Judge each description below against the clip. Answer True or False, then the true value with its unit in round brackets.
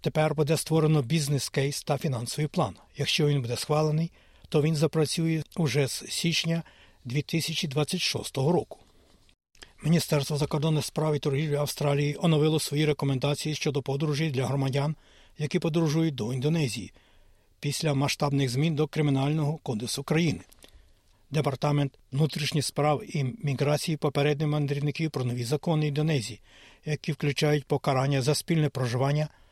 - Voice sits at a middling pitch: True (150 Hz)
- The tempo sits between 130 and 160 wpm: False (120 wpm)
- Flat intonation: True (2.0 semitones)